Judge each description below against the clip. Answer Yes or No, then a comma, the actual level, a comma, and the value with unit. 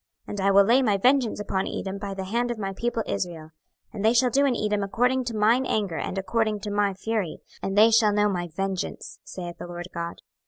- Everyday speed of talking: No, fast, 235 wpm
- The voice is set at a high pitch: Yes, high, 205 Hz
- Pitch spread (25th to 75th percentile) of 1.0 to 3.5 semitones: Yes, average, 3.0 semitones